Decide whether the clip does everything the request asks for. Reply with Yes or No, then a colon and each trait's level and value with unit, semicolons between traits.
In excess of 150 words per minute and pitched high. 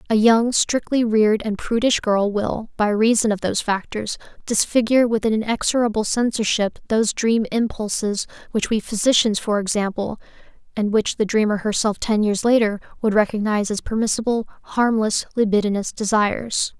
No: average, 145 wpm; high, 215 Hz